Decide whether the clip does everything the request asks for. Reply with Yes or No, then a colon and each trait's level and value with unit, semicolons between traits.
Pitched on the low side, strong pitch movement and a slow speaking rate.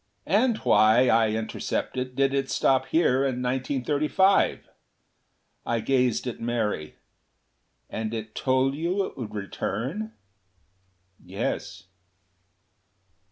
No: low, 130 Hz; average, 3.5 semitones; slow, 100 wpm